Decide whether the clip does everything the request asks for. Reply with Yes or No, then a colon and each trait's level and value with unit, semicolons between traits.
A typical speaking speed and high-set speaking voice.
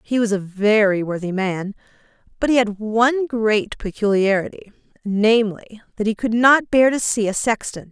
Yes: average, 160 wpm; high, 215 Hz